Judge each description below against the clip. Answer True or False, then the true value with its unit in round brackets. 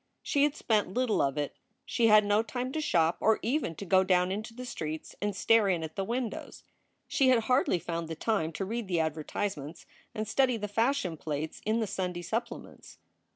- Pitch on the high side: True (205 Hz)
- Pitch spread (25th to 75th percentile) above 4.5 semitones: True (5.5 semitones)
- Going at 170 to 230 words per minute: True (200 wpm)